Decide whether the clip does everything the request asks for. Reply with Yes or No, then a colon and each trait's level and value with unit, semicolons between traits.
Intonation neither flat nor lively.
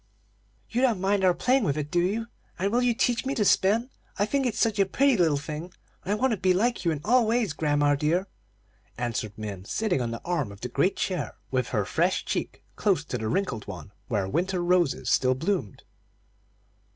No: wide, 7.6 semitones